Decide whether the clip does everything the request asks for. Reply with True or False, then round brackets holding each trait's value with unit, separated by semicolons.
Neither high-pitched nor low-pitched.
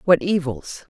True (170 Hz)